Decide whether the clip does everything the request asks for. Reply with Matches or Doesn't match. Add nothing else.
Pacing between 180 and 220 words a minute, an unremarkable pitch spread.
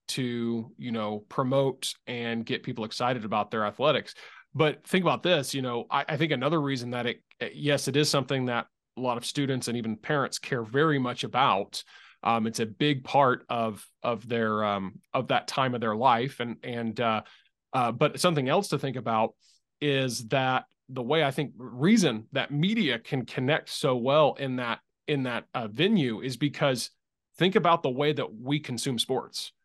Matches